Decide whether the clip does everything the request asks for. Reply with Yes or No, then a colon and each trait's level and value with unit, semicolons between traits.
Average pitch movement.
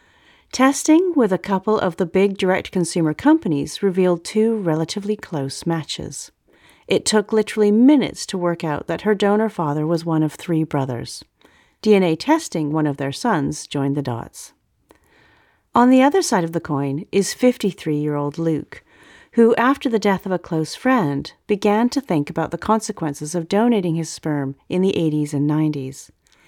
No: wide, 5.9 semitones